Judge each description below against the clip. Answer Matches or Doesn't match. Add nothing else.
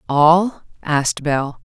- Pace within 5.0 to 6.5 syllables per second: Doesn't match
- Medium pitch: Matches